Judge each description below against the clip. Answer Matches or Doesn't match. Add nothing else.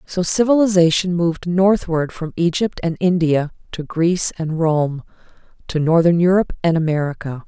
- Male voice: Doesn't match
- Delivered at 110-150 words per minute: Matches